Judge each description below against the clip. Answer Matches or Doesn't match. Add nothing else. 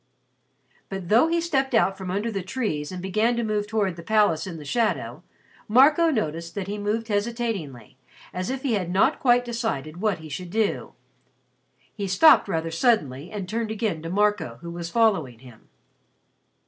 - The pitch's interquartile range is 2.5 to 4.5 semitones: Doesn't match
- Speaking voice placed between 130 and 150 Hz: Doesn't match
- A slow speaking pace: Doesn't match